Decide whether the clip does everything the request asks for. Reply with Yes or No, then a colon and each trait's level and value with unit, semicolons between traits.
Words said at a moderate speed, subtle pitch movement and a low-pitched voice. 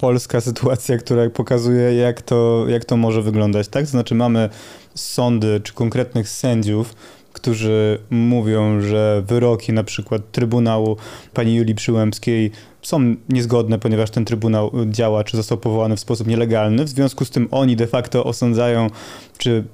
Yes: average, 145 wpm; narrow, 1.8 semitones; low, 115 Hz